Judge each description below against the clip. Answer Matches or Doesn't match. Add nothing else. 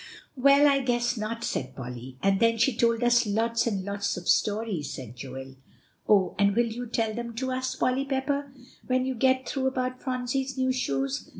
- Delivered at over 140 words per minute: Matches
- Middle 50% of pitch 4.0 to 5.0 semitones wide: Matches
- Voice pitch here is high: Matches